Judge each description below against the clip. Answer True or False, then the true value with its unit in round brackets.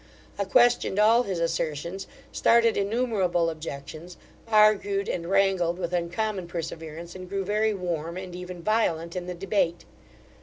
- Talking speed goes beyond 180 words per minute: False (140 wpm)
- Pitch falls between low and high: True (180 Hz)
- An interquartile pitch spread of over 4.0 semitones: False (3.4 semitones)